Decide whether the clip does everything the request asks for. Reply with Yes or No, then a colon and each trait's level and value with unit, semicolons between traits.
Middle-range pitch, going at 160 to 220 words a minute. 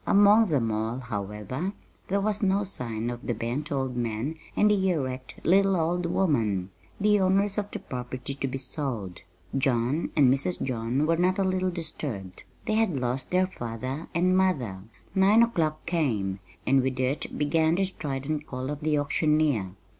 Yes: medium, 145 Hz; average, 170 wpm